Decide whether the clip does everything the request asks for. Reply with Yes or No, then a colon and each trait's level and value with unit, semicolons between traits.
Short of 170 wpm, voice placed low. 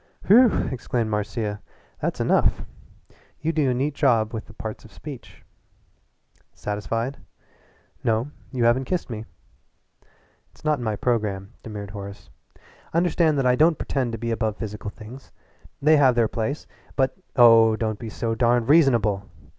Yes: average, 155 wpm; low, 115 Hz